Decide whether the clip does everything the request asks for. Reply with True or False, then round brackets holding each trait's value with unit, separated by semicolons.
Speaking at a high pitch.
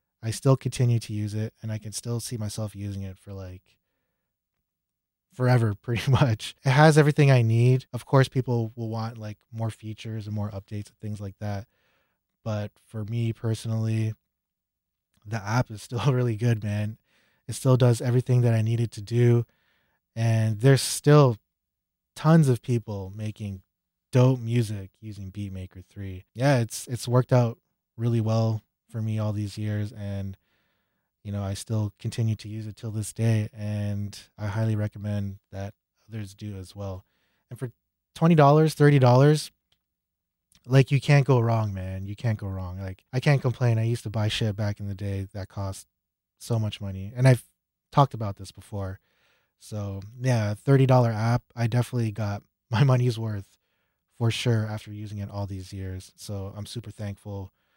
False (110 Hz)